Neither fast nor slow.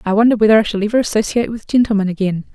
No: fast, 235 wpm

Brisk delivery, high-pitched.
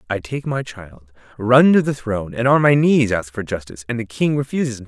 No: fast, 245 wpm; low, 120 Hz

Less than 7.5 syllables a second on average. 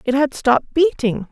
Yes: 5.0 syllables/s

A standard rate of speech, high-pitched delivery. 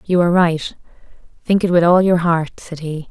No: average, 195 wpm; medium, 170 Hz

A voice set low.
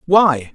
No: medium, 160 Hz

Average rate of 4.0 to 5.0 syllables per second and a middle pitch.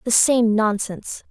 No: 4.4 syllables/s; high, 225 Hz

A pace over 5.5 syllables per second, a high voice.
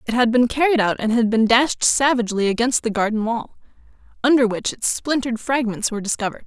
Yes: 6.2 syllables/s; high, 235 Hz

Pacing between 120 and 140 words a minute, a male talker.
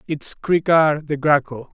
Yes: slow, 135 wpm; male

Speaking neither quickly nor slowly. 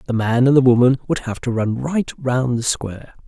No: fast, 240 wpm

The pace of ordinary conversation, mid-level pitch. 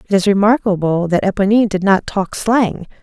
No: average, 180 wpm; high, 200 Hz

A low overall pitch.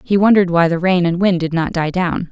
No: medium, 175 Hz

